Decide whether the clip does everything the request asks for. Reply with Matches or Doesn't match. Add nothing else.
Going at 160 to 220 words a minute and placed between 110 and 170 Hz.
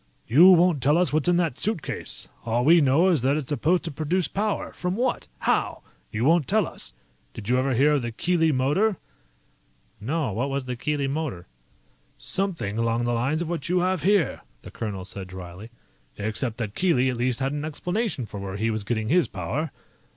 Matches